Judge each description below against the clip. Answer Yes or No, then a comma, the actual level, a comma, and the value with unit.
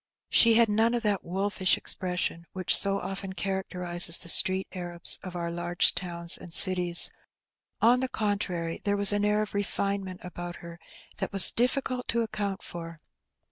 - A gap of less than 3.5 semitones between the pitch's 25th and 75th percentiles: Yes, average, 2.9 semitones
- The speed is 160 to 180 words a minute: Yes, average, 165 wpm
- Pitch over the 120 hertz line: Yes, high, 190 Hz